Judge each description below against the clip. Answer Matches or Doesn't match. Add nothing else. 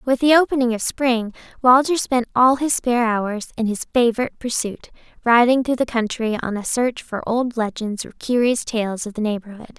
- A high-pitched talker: Matches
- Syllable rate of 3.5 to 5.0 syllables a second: Doesn't match